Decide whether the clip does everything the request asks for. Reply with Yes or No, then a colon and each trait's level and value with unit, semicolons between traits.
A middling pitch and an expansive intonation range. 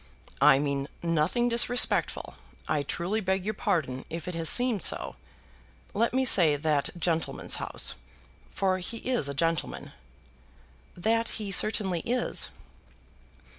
Yes: medium, 180 Hz; wide, 6.0 semitones